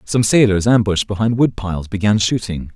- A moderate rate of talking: Yes, average, 175 wpm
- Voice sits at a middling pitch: No, low, 105 Hz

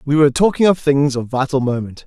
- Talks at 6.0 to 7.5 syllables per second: Yes, 6.2 syllables/s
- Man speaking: Yes, male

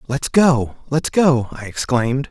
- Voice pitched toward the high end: No, low, 135 Hz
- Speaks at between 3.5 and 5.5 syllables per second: Yes, 4.0 syllables/s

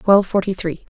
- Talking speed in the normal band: Yes, average, 190 wpm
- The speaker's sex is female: Yes, female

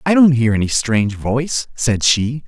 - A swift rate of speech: No, average, 195 wpm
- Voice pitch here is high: No, low, 125 Hz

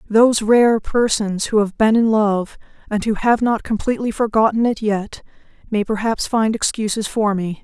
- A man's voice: No, female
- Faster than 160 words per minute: Yes, average, 175 wpm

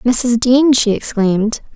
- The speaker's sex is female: Yes, female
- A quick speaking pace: No, slow, 135 wpm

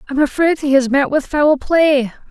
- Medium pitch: No, very high, 285 Hz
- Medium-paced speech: No, fast, 210 wpm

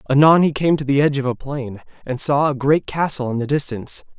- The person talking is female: No, male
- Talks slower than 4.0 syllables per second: No, 6.1 syllables/s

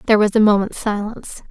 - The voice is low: No, high, 210 Hz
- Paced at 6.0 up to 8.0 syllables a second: Yes, 6.9 syllables/s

